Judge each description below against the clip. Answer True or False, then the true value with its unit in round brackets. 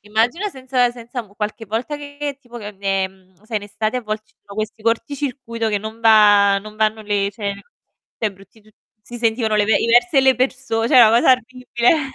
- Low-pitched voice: False (225 Hz)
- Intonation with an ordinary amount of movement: True (3.1 semitones)